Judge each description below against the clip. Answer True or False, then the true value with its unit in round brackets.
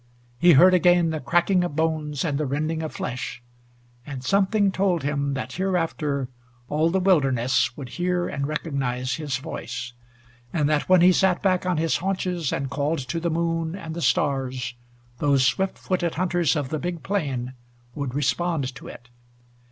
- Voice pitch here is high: False (155 Hz)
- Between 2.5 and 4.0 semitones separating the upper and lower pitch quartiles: False (4.4 semitones)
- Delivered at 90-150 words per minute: False (170 wpm)